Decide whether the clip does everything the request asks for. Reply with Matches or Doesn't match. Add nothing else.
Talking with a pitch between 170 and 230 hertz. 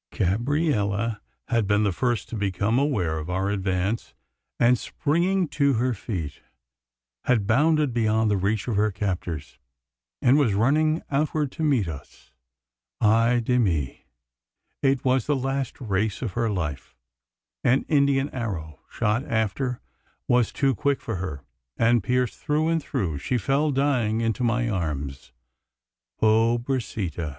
Doesn't match